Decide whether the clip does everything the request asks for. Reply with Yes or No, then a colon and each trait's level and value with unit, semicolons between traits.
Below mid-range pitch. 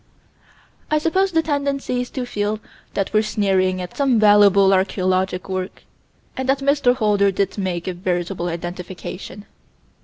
No: high, 200 Hz